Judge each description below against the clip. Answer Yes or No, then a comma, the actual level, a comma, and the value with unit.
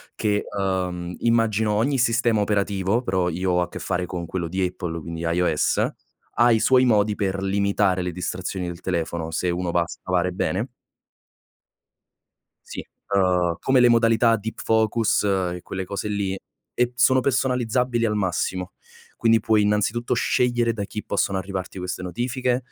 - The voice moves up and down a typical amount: Yes, average, 4.1 semitones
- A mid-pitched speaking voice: No, low, 100 Hz